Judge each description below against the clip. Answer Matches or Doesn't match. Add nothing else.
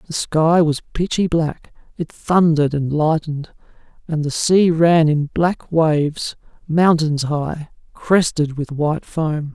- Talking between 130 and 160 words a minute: Matches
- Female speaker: Doesn't match